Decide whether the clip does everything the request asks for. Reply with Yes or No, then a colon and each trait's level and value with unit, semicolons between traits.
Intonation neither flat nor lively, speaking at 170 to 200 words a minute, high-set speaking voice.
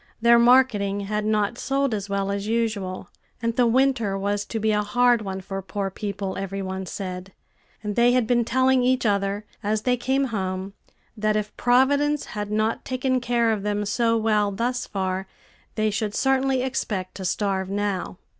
Yes: average, 3.5 semitones; average, 180 wpm; high, 215 Hz